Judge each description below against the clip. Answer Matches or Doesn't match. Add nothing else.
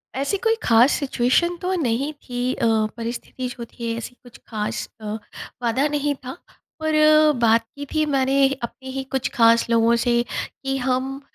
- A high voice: Matches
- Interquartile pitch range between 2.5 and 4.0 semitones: Matches